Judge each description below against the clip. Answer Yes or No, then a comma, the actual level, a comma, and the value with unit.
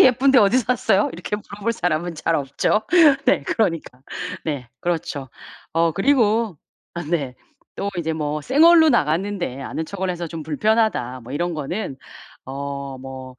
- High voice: No, medium, 170 Hz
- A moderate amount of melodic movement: No, wide, 6.8 semitones